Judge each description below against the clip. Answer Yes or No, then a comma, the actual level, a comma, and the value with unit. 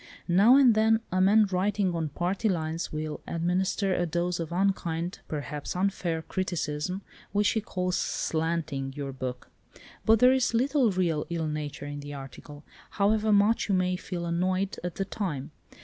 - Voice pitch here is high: No, medium, 180 Hz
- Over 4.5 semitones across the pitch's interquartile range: No, average, 4.1 semitones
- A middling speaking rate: Yes, average, 165 wpm